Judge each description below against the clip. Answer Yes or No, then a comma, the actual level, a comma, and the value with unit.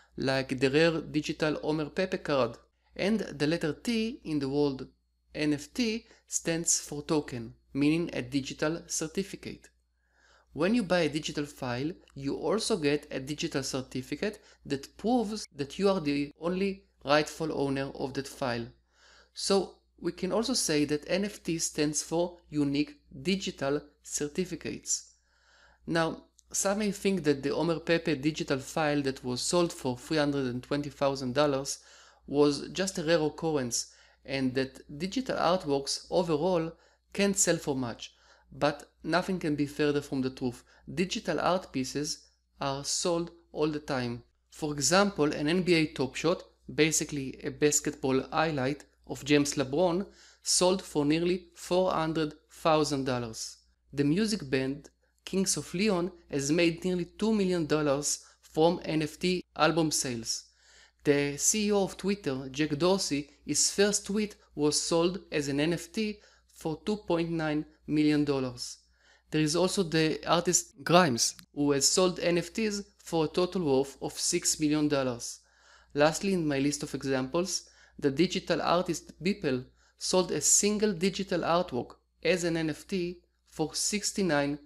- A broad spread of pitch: No, average, 4.1 semitones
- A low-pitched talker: No, medium, 155 Hz